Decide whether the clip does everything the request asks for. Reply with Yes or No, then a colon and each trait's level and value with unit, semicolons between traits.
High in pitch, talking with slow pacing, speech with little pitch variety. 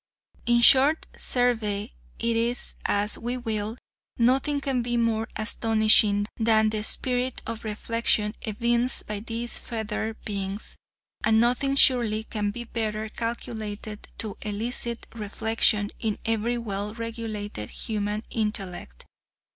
Yes: high, 225 Hz; slow, 115 wpm; narrow, 2.1 semitones